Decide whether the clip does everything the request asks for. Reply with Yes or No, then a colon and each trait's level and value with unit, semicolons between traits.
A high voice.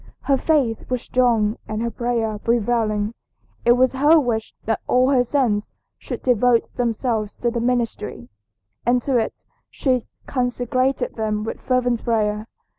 Yes: high, 240 Hz